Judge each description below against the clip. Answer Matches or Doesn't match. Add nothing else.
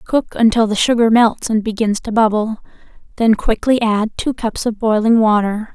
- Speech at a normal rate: Matches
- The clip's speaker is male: Doesn't match